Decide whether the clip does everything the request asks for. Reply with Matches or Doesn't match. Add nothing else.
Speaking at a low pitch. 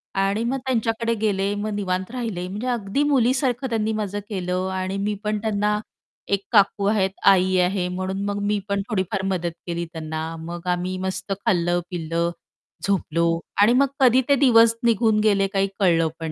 Doesn't match